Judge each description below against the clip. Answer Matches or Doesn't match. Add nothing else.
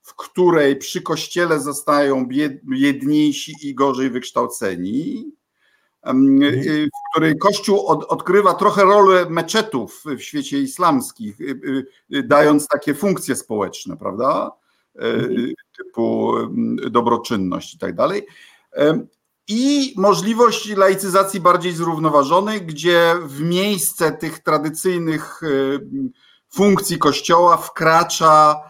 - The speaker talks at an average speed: Doesn't match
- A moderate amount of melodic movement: Doesn't match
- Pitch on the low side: Doesn't match